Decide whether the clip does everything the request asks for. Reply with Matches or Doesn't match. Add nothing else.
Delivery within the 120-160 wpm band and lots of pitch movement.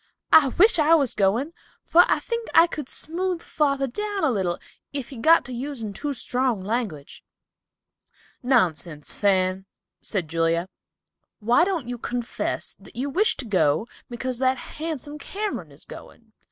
Matches